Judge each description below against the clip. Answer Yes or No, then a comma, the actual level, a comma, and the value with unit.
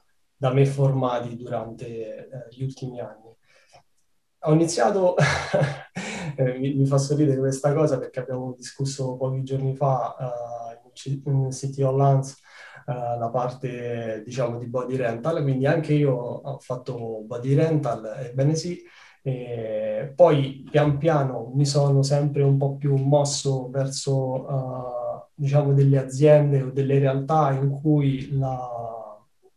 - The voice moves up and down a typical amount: No, narrow, 2.3 semitones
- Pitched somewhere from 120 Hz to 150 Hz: Yes, low, 135 Hz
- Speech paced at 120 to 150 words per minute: Yes, average, 135 wpm